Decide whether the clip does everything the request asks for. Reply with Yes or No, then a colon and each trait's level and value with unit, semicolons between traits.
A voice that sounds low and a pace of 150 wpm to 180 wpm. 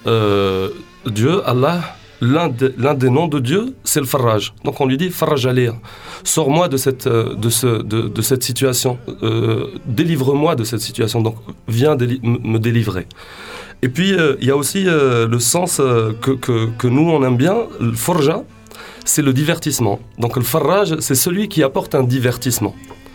Yes: low, 130 Hz; average, 175 wpm